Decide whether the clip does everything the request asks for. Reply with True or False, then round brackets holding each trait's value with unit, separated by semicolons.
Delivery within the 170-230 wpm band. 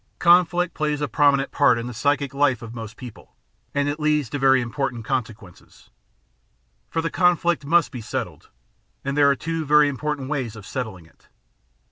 True (180 wpm)